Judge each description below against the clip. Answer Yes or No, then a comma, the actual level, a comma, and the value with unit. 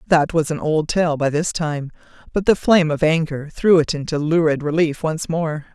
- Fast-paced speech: Yes, fast, 210 wpm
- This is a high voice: No, medium, 160 Hz